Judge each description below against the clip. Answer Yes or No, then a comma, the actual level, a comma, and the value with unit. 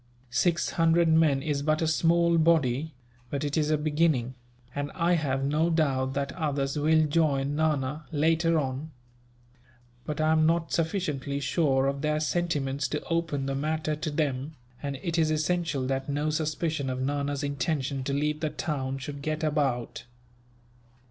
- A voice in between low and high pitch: Yes, medium, 150 Hz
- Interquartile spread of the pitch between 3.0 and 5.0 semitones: No, narrow, 2.4 semitones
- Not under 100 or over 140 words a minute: No, average, 160 wpm